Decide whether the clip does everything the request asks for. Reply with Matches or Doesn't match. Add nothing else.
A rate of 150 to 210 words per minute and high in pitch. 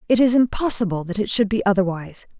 Matches